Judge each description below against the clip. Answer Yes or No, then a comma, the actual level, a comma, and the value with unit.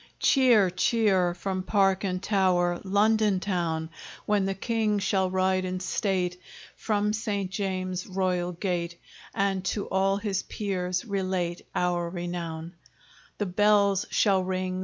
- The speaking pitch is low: No, high, 190 Hz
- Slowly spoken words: Yes, slow, 130 wpm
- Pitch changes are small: Yes, narrow, 2.0 semitones